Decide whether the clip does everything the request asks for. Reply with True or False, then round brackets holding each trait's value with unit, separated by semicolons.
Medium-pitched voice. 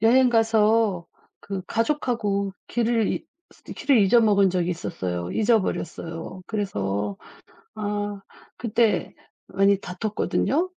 False (205 Hz)